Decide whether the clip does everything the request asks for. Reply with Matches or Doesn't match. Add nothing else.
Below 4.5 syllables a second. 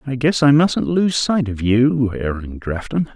Matches